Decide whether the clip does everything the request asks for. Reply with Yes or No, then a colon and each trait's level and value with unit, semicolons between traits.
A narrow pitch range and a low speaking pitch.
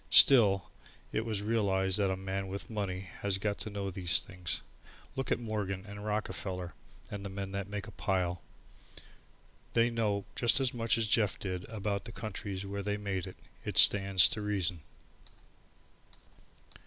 Yes: narrow, 2.0 semitones; low, 100 Hz